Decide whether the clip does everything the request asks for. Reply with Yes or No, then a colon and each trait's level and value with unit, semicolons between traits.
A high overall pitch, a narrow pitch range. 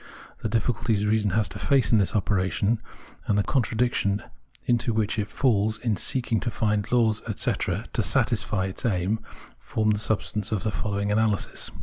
No: low, 110 Hz; narrow, 1.9 semitones